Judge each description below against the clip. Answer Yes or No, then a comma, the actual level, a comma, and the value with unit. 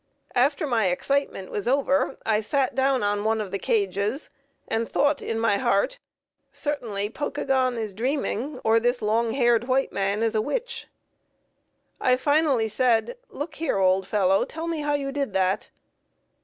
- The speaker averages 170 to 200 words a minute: No, average, 160 wpm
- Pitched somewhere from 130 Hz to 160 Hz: No, high, 240 Hz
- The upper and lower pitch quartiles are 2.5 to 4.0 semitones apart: No, average, 5.1 semitones